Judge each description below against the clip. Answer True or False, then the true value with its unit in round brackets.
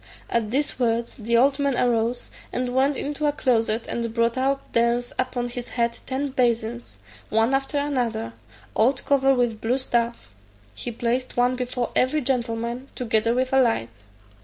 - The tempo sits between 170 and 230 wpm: False (160 wpm)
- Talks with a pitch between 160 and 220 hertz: False (245 Hz)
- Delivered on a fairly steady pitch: True (2.2 semitones)